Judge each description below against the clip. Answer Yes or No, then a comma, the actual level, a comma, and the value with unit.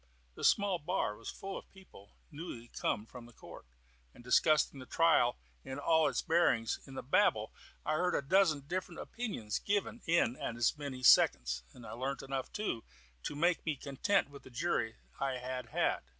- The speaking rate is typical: Yes, average, 180 wpm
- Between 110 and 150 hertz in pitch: Yes, medium, 140 Hz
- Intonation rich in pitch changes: Yes, wide, 5.8 semitones